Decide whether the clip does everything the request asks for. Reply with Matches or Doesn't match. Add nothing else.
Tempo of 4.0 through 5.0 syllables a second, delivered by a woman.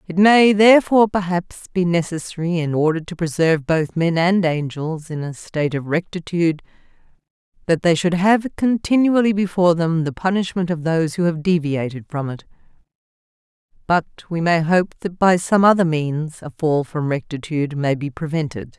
Doesn't match